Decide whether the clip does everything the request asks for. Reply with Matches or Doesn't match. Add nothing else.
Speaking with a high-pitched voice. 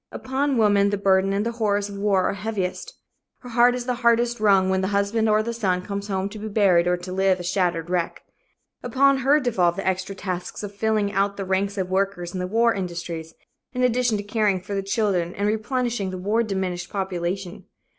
Matches